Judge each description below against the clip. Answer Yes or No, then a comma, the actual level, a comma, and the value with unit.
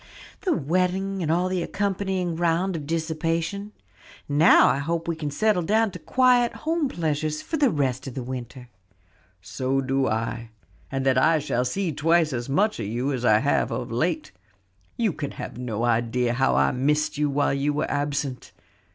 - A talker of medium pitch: Yes, medium, 150 Hz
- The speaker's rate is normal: Yes, average, 180 wpm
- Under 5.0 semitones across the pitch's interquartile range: No, wide, 5.6 semitones